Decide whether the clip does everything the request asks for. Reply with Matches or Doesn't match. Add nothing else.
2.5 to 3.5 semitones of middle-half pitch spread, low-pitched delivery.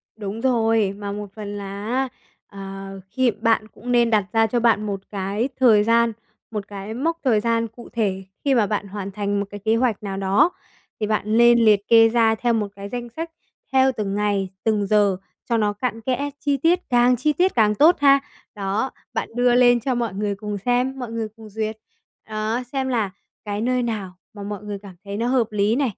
Doesn't match